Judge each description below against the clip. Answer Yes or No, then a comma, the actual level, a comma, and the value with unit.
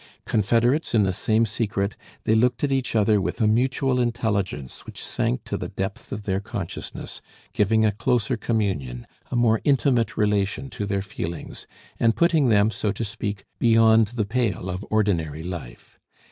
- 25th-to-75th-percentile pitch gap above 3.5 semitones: No, average, 3.0 semitones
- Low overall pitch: Yes, low, 110 Hz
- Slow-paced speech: No, average, 165 wpm